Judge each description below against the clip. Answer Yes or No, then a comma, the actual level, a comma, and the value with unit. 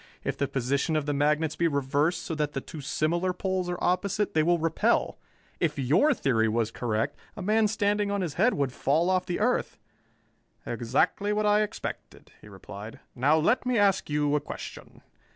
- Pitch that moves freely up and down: Yes, wide, 6.0 semitones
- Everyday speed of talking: Yes, average, 190 wpm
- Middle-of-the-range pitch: Yes, medium, 160 Hz